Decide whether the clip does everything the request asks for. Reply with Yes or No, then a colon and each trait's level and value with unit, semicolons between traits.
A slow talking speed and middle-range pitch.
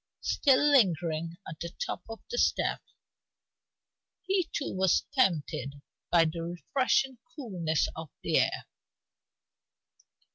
Yes: slow, 110 wpm; medium, 175 Hz